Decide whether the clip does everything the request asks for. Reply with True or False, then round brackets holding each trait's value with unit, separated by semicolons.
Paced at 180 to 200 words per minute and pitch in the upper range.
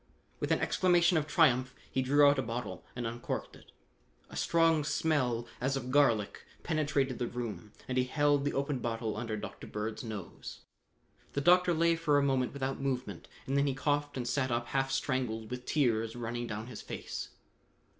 False (185 wpm; 130 Hz)